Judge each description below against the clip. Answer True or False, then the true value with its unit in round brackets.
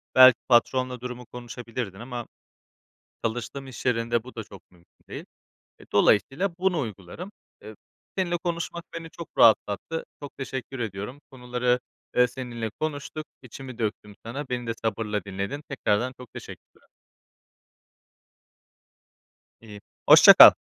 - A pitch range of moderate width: True (3.3 semitones)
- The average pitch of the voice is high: False (125 Hz)